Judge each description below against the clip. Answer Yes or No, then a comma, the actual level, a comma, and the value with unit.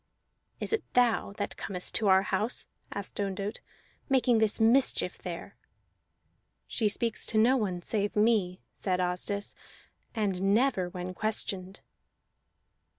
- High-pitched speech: Yes, high, 205 Hz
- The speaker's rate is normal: No, slow, 125 wpm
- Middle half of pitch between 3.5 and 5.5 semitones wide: No, average, 3.1 semitones